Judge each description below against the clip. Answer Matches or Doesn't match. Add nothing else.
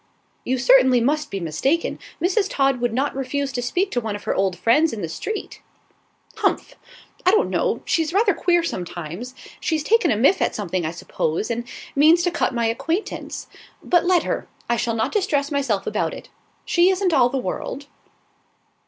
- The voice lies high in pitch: Matches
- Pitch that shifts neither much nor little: Doesn't match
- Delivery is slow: Doesn't match